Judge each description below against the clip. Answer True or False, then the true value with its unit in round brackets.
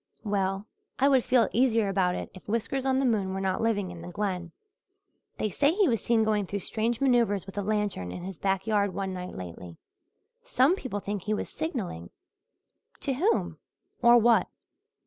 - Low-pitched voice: False (210 Hz)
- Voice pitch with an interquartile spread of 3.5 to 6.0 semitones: True (4.0 semitones)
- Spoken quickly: False (185 wpm)